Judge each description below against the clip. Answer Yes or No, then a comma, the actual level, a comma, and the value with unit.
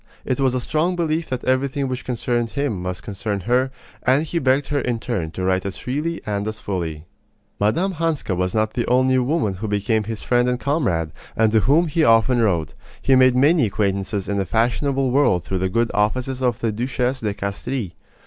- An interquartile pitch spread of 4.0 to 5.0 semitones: Yes, average, 4.7 semitones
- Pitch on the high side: No, low, 120 Hz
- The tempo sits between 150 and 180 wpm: No, fast, 205 wpm